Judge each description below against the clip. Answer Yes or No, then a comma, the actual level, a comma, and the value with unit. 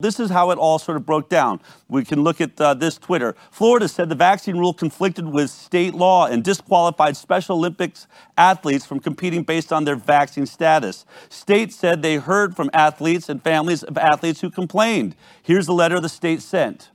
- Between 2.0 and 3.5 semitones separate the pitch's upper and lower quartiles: Yes, average, 2.8 semitones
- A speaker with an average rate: Yes, average, 195 wpm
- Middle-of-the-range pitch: Yes, medium, 165 Hz